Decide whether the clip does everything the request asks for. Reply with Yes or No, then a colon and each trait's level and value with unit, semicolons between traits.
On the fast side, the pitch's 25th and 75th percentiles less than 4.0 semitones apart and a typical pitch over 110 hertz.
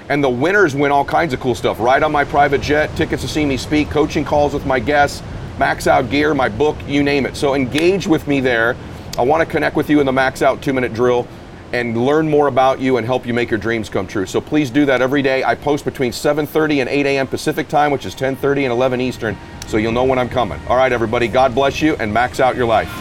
Yes: fast, 260 wpm; average, 2.8 semitones; low, 135 Hz